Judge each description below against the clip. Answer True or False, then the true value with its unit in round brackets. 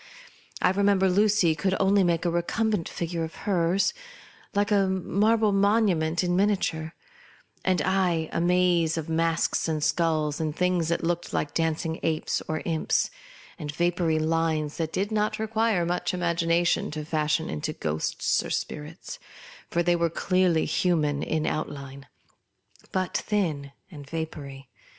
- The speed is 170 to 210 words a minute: False (150 wpm)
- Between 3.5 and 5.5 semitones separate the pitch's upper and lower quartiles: False (3.0 semitones)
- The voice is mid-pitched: True (170 Hz)